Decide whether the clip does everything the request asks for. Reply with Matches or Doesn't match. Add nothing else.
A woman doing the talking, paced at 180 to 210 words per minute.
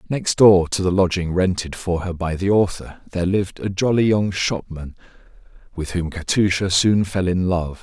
Doesn't match